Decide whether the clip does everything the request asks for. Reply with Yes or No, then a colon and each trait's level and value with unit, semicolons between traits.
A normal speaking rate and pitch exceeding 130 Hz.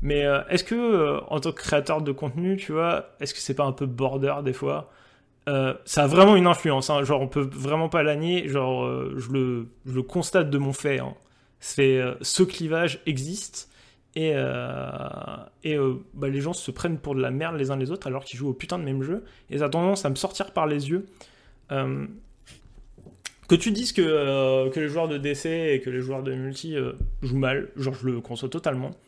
No: fast, 230 wpm; medium, 140 Hz